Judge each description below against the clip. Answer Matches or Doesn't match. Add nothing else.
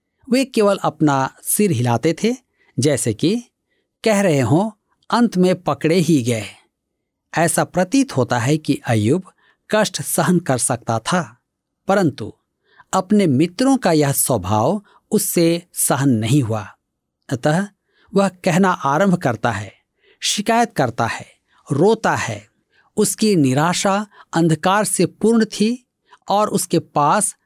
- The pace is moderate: Matches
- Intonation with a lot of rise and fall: Matches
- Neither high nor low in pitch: Matches